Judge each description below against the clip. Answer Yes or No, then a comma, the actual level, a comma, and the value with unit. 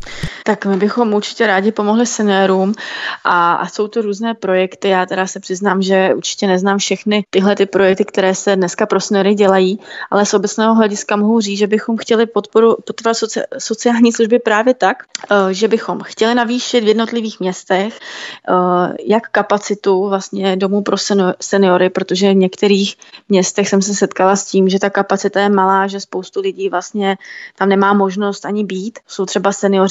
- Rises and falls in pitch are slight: Yes, narrow, 2.0 semitones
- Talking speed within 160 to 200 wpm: Yes, fast, 170 wpm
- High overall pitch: Yes, high, 200 Hz